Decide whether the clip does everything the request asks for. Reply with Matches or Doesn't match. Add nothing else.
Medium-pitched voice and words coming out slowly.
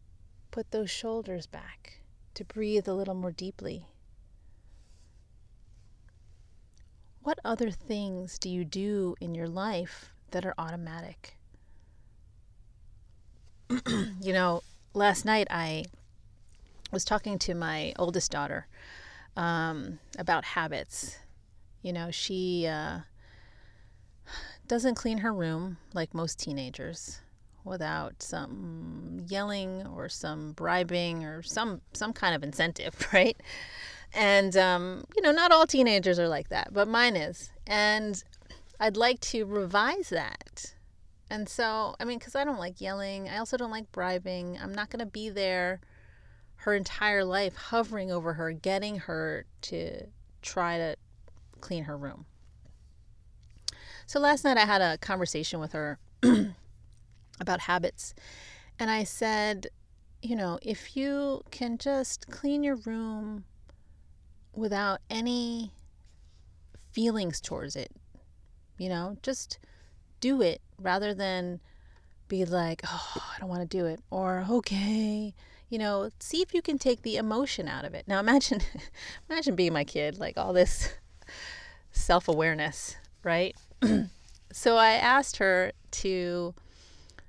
Matches